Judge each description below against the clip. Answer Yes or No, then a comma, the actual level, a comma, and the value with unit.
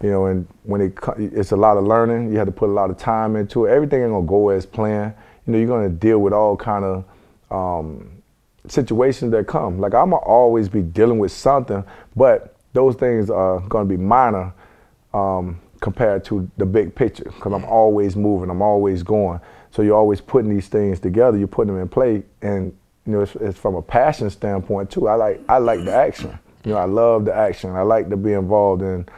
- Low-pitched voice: Yes, low, 105 Hz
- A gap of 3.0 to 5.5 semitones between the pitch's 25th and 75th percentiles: No, narrow, 2.4 semitones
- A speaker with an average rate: No, fast, 220 wpm